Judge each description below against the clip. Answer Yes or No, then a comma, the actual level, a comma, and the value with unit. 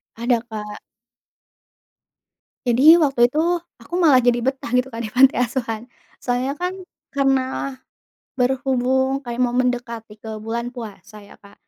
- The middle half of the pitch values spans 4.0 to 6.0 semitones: No, narrow, 2.4 semitones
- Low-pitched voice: No, high, 245 Hz